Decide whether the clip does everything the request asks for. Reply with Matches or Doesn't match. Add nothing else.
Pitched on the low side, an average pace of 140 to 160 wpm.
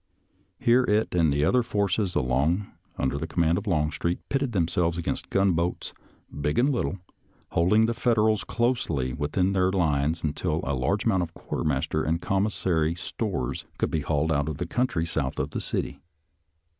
Doesn't match